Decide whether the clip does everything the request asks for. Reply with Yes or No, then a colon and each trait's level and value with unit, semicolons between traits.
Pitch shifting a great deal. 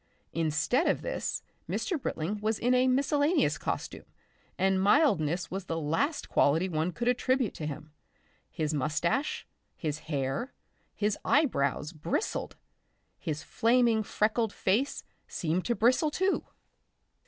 Yes: wide, 8.3 semitones